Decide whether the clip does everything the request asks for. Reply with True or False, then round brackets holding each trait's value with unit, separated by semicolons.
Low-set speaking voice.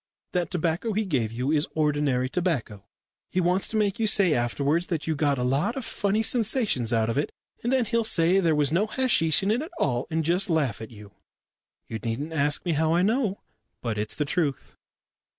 False (160 Hz)